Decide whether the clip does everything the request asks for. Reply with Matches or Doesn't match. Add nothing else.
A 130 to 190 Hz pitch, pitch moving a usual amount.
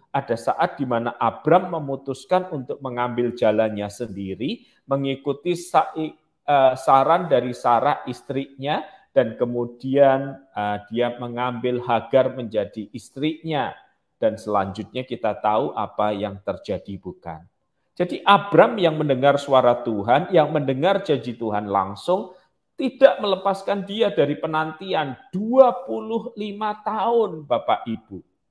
Doesn't match